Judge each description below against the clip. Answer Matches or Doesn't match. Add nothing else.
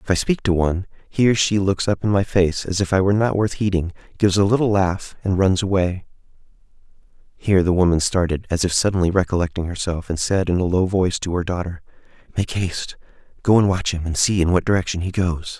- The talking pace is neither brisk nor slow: Doesn't match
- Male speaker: Matches